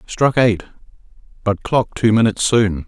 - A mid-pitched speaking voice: No, low, 110 Hz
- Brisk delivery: No, average, 145 wpm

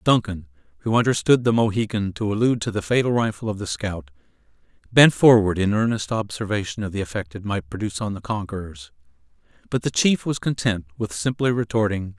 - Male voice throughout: Yes, male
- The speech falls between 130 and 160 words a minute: No, average, 175 wpm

